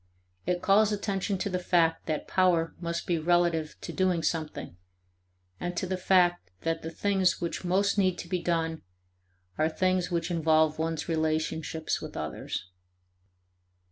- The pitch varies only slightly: Yes, narrow, 2.3 semitones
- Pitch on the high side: No, medium, 175 Hz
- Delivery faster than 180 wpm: No, average, 150 wpm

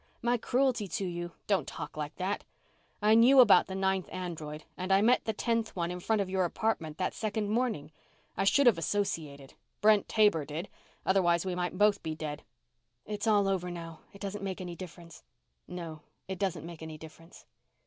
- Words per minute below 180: No, average, 190 wpm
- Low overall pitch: No, medium, 185 Hz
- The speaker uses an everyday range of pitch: Yes, average, 3.9 semitones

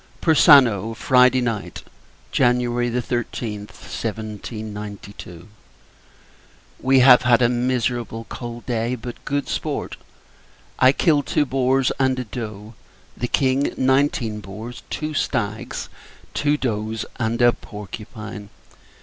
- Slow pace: Yes, slow, 110 wpm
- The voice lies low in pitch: Yes, low, 120 Hz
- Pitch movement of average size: Yes, average, 3.0 semitones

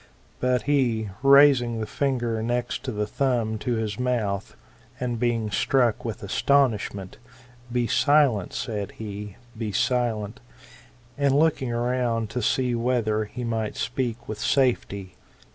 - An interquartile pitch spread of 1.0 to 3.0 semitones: Yes, average, 2.7 semitones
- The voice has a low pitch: Yes, low, 120 Hz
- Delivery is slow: Yes, slow, 130 wpm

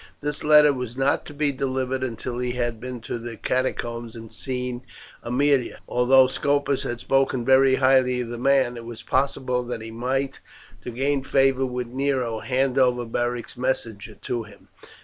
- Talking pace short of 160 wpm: No, average, 175 wpm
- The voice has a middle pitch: No, low, 125 Hz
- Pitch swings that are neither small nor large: No, narrow, 1.9 semitones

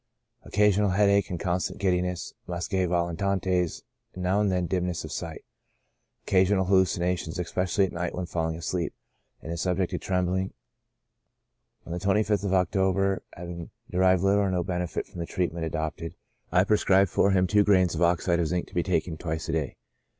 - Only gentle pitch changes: Yes, narrow, 1.9 semitones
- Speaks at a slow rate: No, average, 170 wpm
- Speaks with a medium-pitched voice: No, very low, 90 Hz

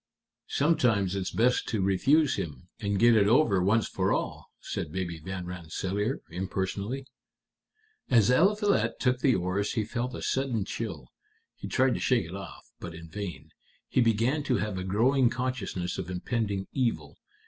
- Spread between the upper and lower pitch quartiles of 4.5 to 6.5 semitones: Yes, average, 5.2 semitones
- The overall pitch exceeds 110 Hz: No, low, 105 Hz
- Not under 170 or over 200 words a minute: No, average, 160 wpm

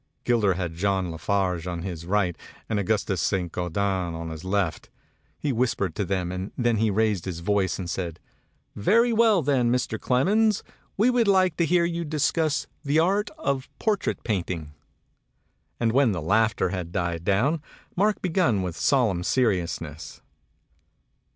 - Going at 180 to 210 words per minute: No, average, 155 wpm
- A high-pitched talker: No, low, 105 Hz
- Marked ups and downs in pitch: Yes, wide, 8.3 semitones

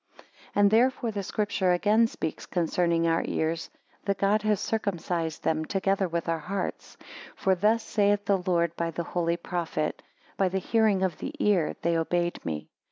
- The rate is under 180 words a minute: Yes, average, 165 wpm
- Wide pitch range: No, average, 3.4 semitones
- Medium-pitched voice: Yes, medium, 180 Hz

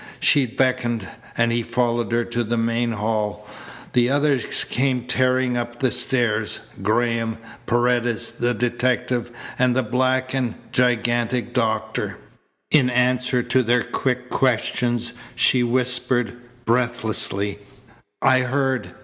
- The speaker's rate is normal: No, slow, 120 wpm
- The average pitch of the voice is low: Yes, low, 120 Hz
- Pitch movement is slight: Yes, narrow, 1.5 semitones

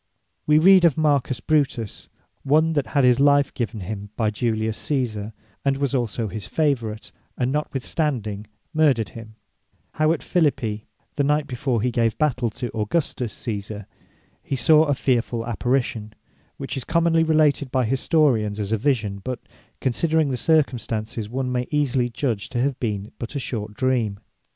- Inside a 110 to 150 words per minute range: No, average, 160 wpm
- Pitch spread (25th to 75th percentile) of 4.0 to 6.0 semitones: Yes, average, 4.6 semitones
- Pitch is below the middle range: Yes, low, 125 Hz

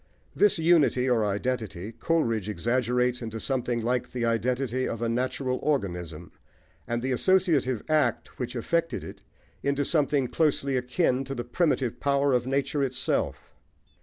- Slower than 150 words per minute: Yes, average, 140 wpm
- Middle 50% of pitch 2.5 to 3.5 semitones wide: Yes, average, 3.0 semitones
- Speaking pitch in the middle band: No, low, 125 Hz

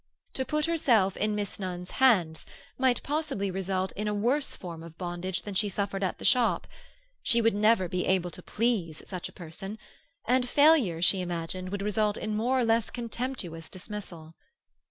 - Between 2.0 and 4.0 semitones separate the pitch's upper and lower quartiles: No, average, 4.6 semitones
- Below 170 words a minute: No, average, 175 wpm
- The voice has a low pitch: No, high, 205 Hz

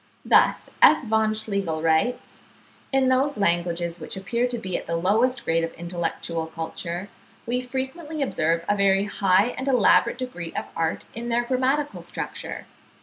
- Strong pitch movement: Yes, wide, 6.7 semitones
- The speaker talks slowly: No, average, 155 wpm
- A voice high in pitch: Yes, high, 205 Hz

